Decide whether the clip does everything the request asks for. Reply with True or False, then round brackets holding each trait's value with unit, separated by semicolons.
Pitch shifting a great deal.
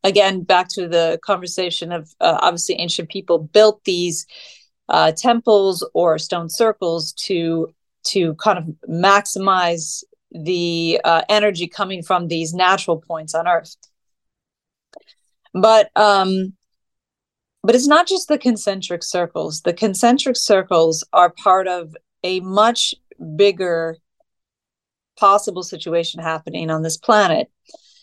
False (3.9 semitones)